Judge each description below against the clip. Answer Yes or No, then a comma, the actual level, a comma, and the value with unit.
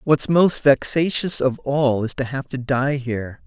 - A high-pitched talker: No, medium, 140 Hz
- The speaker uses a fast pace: No, average, 190 wpm